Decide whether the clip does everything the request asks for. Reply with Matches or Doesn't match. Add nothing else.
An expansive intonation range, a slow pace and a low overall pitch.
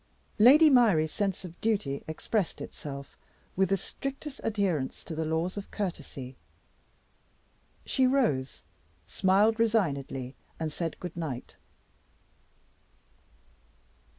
Doesn't match